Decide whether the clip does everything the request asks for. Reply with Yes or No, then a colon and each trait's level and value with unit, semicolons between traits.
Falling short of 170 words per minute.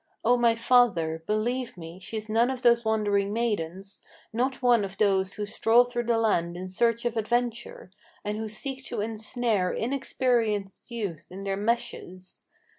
Yes: average, 160 wpm